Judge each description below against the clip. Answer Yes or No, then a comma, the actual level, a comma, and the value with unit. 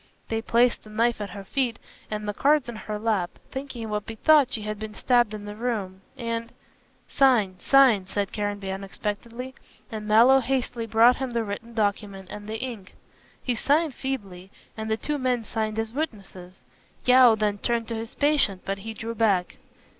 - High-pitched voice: Yes, high, 225 Hz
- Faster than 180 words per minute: Yes, average, 190 wpm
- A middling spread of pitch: Yes, average, 3.0 semitones